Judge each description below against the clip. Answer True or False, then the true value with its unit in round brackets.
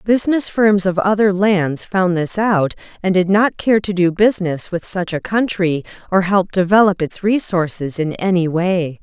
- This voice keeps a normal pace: True (180 wpm)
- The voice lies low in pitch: False (190 Hz)